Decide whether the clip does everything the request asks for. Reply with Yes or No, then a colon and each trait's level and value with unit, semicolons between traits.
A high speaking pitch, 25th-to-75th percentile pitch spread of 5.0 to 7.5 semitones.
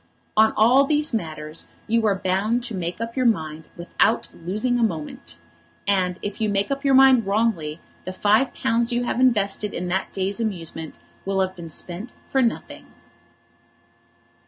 No: high, 205 Hz; average, 4.5 semitones